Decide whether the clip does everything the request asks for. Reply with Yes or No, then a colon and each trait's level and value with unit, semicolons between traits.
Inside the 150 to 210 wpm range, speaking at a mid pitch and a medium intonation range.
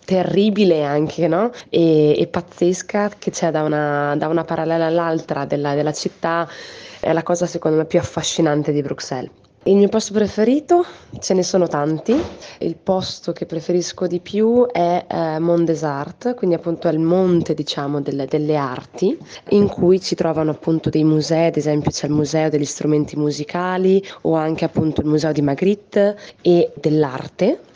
Yes: fast, 170 wpm; medium, 165 Hz; average, 3.3 semitones